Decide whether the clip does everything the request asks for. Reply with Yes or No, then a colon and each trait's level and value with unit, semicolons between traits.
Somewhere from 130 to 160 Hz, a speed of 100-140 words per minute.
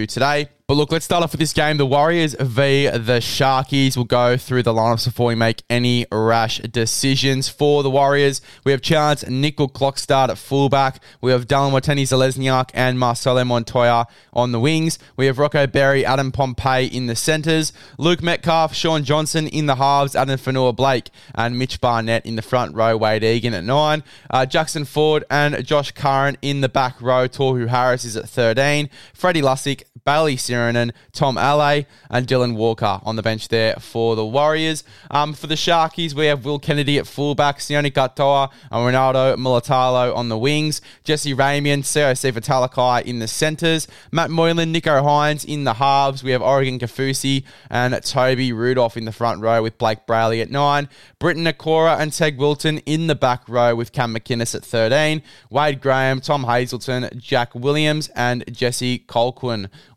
No: low, 135 Hz; average, 180 wpm